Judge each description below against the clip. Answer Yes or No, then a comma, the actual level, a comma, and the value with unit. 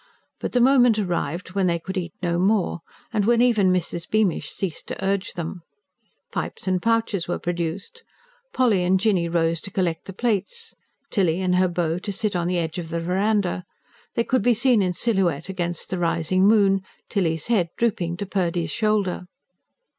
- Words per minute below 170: No, average, 180 wpm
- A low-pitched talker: No, medium, 185 Hz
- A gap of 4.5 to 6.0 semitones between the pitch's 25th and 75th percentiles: No, average, 3.6 semitones